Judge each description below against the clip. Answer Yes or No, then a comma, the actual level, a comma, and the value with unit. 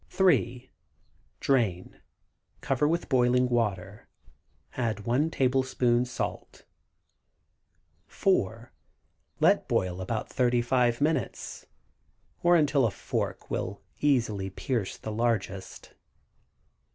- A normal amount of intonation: Yes, average, 3.6 semitones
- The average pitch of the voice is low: Yes, low, 120 Hz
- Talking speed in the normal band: No, slow, 90 wpm